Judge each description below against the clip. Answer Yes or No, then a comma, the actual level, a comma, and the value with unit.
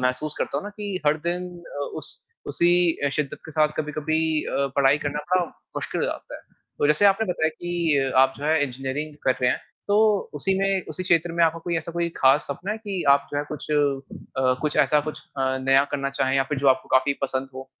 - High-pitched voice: No, medium, 150 Hz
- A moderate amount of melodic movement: Yes, average, 3.9 semitones